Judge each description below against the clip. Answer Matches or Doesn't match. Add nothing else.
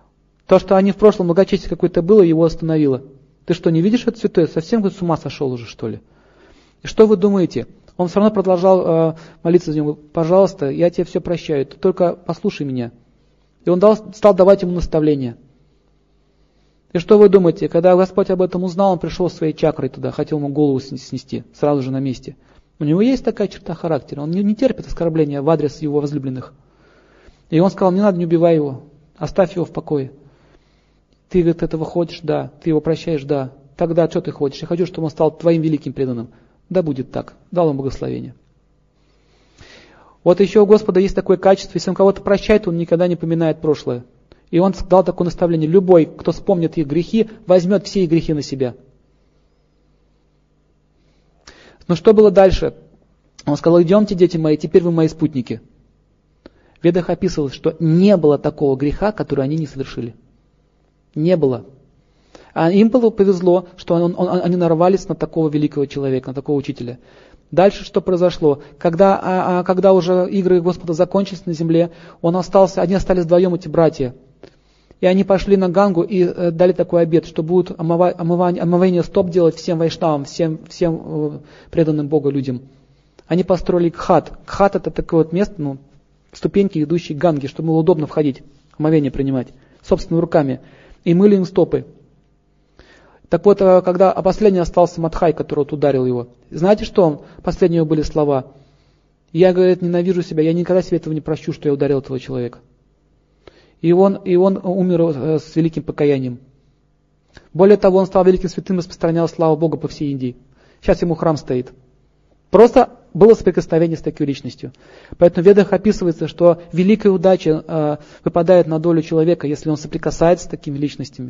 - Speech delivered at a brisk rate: Matches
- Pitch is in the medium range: Matches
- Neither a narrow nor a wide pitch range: Matches